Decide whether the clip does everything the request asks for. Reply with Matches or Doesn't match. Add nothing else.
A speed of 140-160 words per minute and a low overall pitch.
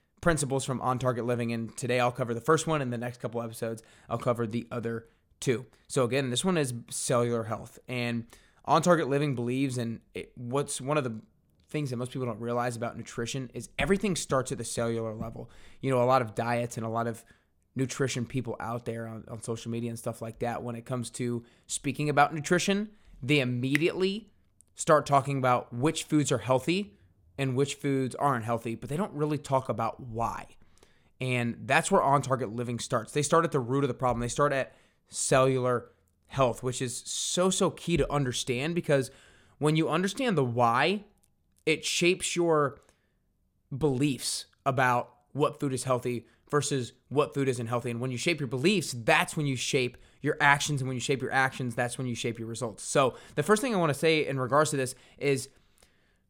Doesn't match